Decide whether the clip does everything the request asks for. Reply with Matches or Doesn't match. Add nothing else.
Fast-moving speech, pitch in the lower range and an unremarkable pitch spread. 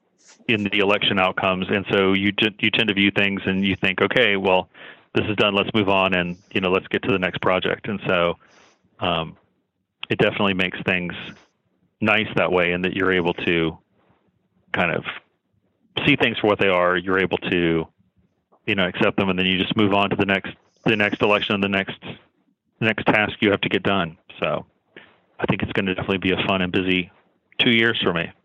Doesn't match